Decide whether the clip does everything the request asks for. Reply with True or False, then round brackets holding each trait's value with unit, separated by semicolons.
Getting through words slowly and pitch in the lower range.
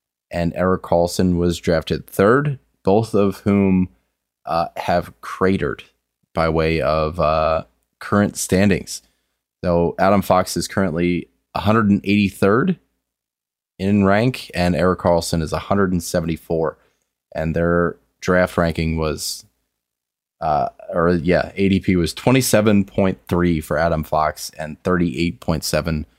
True (110 wpm; 90 Hz)